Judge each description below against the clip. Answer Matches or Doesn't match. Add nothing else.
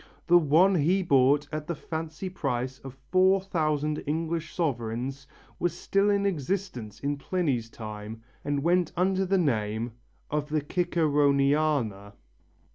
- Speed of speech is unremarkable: Doesn't match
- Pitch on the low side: Doesn't match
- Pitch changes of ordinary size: Matches